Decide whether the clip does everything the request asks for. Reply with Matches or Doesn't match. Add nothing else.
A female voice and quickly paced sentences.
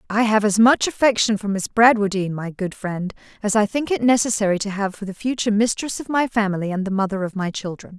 Matches